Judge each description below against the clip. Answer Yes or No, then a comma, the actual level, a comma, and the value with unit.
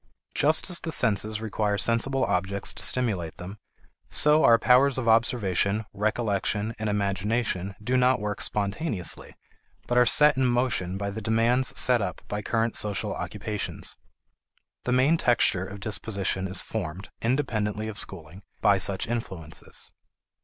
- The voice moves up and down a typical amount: Yes, average, 3.6 semitones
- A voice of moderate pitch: No, low, 110 Hz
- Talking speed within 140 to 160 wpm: Yes, average, 145 wpm